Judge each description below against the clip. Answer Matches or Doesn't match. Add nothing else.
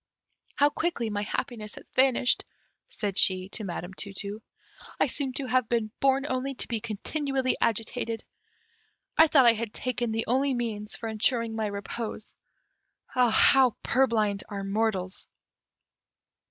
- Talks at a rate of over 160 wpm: Doesn't match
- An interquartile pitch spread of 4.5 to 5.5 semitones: Doesn't match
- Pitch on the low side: Doesn't match